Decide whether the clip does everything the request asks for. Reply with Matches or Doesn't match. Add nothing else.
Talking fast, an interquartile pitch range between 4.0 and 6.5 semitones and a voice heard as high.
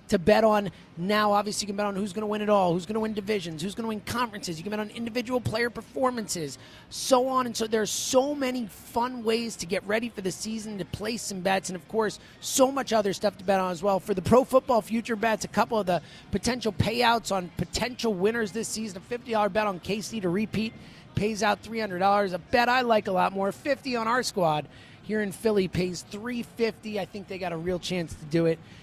Doesn't match